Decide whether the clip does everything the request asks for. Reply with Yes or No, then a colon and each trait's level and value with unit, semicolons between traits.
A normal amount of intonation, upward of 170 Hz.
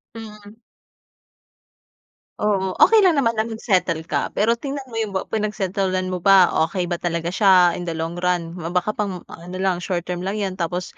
Yes: average, 3.2 semitones; high, 190 Hz